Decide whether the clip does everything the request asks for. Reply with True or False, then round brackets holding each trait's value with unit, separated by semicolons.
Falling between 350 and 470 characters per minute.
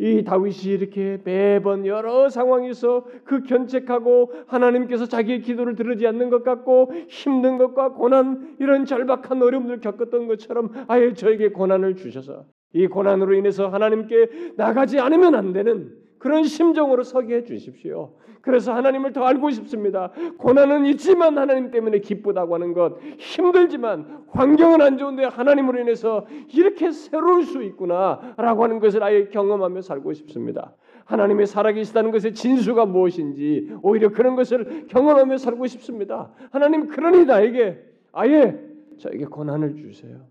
True (360 characters per minute)